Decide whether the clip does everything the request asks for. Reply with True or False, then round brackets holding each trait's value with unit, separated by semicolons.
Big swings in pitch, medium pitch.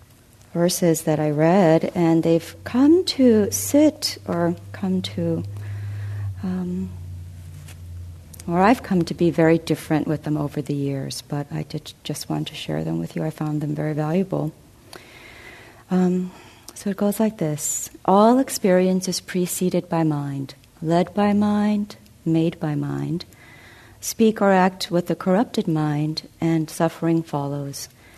True (7.3 semitones; 155 Hz)